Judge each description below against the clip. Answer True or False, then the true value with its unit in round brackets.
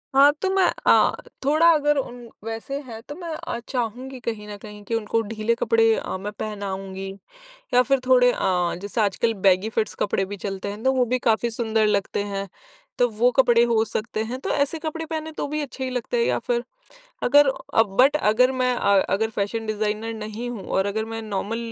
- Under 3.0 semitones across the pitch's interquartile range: False (3.8 semitones)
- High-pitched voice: True (230 Hz)